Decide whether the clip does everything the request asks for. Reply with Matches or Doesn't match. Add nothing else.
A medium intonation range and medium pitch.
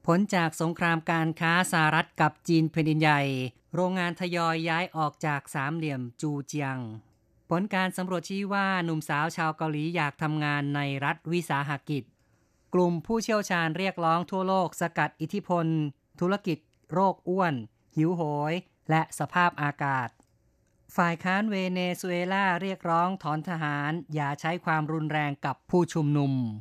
Matches